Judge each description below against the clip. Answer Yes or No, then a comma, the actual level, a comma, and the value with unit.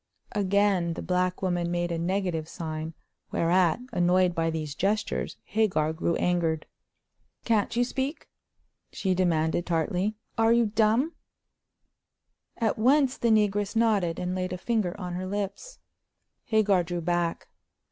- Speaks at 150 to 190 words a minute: No, slow, 135 wpm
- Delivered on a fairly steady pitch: No, average, 3.8 semitones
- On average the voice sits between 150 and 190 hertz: Yes, medium, 185 Hz